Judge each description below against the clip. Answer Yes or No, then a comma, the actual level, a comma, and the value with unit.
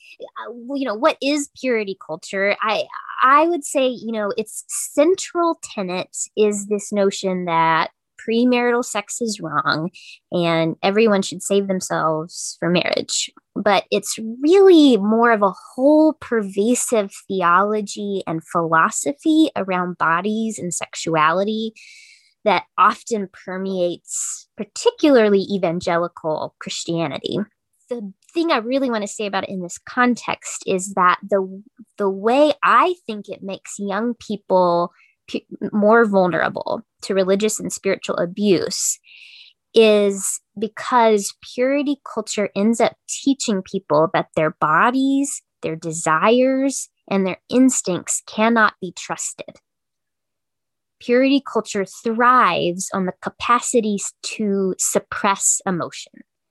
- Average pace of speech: No, slow, 115 wpm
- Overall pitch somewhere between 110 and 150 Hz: No, high, 210 Hz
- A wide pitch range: No, average, 4.6 semitones